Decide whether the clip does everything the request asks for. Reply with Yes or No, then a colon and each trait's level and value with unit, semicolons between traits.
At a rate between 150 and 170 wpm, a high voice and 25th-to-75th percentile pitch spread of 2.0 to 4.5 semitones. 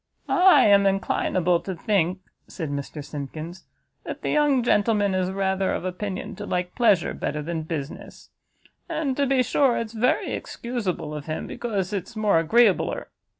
No: average, 155 wpm; high, 195 Hz; wide, 5.4 semitones